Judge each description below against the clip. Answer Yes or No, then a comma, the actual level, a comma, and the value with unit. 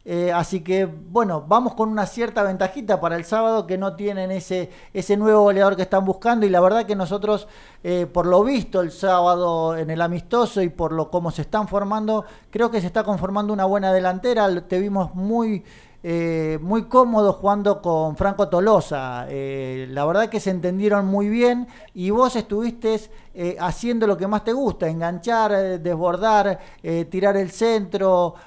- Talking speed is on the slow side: No, average, 180 wpm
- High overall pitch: Yes, high, 195 Hz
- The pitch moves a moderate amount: Yes, average, 3.3 semitones